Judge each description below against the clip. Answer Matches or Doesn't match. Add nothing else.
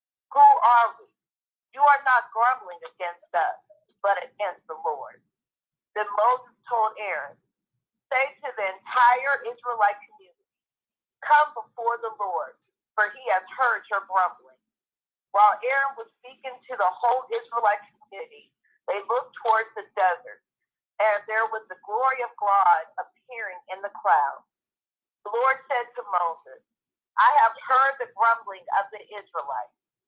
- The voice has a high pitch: Matches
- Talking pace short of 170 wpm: Matches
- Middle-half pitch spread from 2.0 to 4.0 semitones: Doesn't match